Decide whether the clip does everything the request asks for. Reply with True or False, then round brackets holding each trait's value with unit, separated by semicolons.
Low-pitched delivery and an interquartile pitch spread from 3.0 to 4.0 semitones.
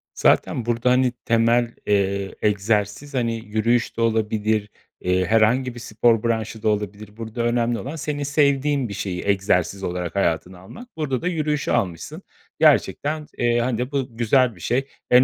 True (115 Hz; 3.6 semitones)